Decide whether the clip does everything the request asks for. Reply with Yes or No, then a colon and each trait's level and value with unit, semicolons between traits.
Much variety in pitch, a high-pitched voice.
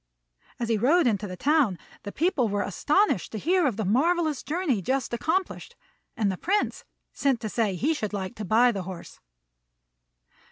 Yes: wide, 7.4 semitones; high, 235 Hz